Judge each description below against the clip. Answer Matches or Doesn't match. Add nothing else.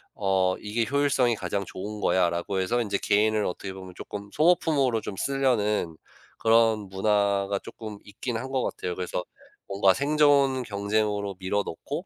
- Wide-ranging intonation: Doesn't match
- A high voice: Doesn't match